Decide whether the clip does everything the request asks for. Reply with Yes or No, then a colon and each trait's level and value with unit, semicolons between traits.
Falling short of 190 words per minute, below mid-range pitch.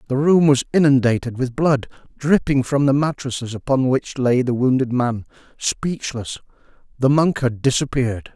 Yes: average, 150 wpm; low, 130 Hz